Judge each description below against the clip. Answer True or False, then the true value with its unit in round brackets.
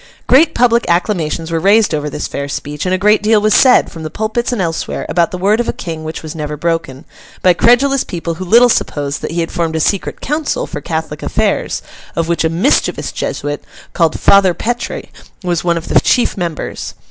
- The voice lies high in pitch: False (175 Hz)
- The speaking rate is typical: False (210 wpm)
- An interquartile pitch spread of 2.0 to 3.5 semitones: False (5.2 semitones)